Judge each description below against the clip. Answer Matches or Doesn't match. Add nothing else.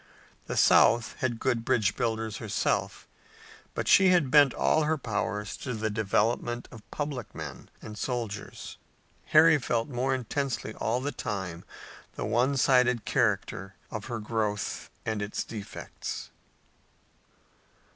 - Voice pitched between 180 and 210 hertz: Doesn't match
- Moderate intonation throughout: Matches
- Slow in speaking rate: Matches